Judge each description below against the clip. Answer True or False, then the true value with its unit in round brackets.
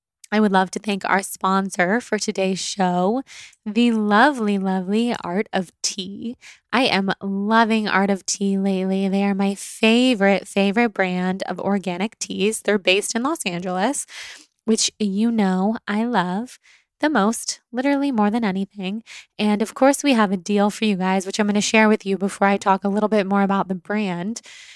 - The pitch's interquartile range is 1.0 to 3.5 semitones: True (2.4 semitones)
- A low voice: False (205 Hz)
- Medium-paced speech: True (180 wpm)